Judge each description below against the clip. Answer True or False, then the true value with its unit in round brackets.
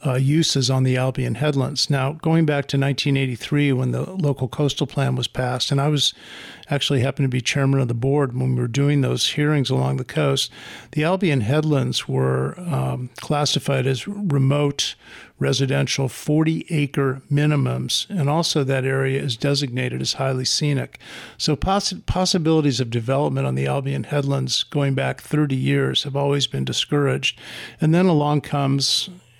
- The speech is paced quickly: False (165 wpm)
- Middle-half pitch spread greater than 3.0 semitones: False (2.4 semitones)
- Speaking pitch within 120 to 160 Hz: True (140 Hz)